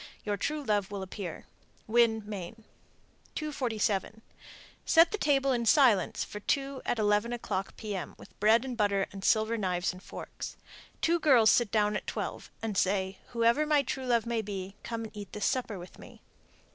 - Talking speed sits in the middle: Yes, average, 175 wpm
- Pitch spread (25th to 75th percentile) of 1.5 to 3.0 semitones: No, average, 3.4 semitones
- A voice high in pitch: Yes, high, 220 Hz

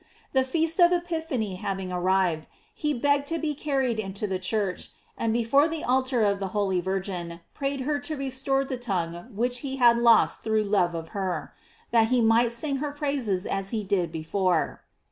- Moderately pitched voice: No, high, 230 Hz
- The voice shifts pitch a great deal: Yes, wide, 6.2 semitones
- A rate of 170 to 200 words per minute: Yes, average, 185 wpm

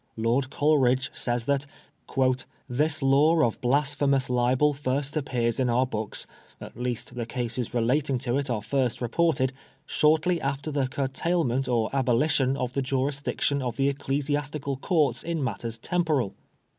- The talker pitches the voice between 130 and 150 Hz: Yes, low, 135 Hz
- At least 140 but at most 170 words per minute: Yes, average, 155 wpm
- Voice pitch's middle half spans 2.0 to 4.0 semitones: Yes, average, 2.9 semitones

